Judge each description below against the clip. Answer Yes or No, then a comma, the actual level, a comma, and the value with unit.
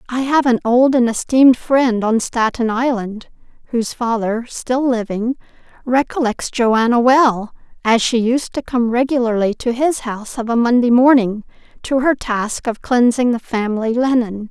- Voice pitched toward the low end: No, high, 240 Hz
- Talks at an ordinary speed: Yes, average, 155 wpm